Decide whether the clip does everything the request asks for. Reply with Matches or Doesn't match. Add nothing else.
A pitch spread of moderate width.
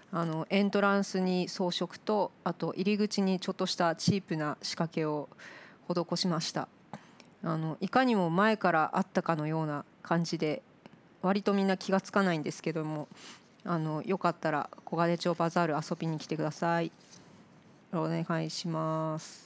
Matches